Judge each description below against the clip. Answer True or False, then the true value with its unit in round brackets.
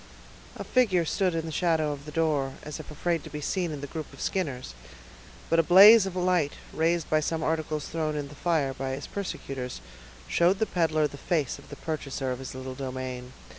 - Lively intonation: False (3.6 semitones)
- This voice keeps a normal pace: False (210 wpm)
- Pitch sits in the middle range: True (155 Hz)